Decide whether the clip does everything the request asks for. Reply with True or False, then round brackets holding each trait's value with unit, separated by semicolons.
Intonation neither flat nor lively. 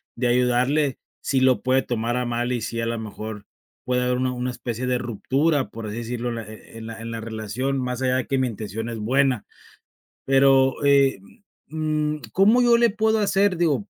True (3.0 semitones)